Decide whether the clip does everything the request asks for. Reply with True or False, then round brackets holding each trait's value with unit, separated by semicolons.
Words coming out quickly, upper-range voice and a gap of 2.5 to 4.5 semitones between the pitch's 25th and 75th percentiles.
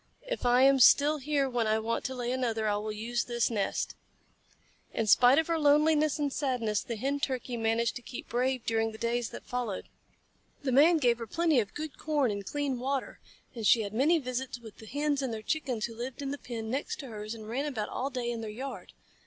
True (225 wpm; 245 Hz; 3.8 semitones)